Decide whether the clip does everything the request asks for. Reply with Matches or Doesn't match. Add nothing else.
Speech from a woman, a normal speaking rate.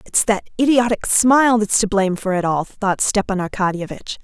Matches